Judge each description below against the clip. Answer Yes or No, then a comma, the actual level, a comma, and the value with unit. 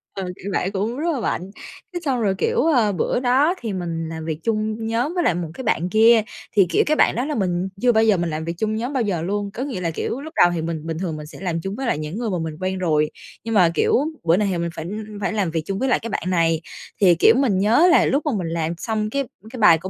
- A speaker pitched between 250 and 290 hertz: No, high, 200 Hz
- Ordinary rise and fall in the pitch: No, wide, 5.7 semitones